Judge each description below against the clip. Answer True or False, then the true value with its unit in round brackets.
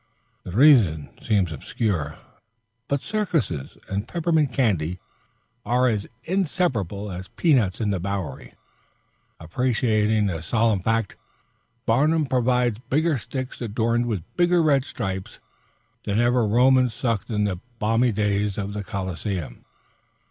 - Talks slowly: True (120 wpm)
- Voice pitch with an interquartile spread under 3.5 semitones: False (4.6 semitones)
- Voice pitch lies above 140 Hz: False (110 Hz)